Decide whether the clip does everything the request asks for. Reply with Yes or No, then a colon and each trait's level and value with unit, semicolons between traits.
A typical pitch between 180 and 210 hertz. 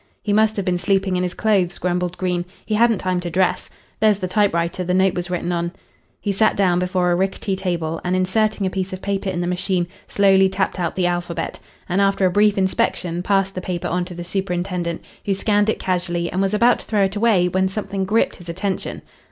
Yes: medium, 185 Hz